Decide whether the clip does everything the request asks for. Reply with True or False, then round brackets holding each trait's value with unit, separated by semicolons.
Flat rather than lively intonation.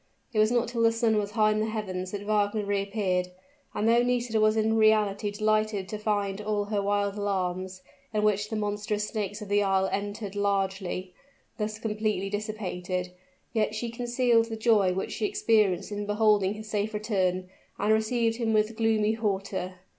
True (1.6 semitones)